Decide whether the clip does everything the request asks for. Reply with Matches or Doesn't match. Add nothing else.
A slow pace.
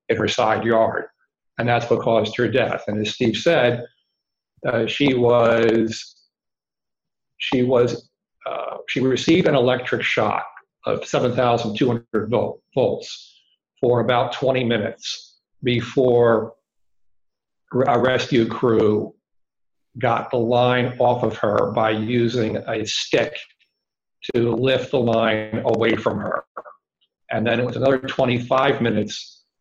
Matches